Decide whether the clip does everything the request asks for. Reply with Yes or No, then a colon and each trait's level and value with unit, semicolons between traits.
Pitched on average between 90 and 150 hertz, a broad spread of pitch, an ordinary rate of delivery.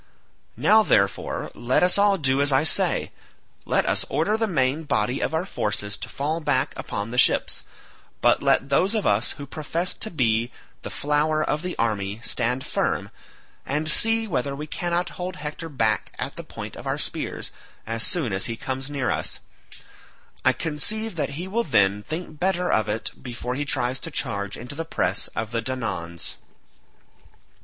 Yes: medium, 140 Hz; wide, 6.4 semitones; average, 180 wpm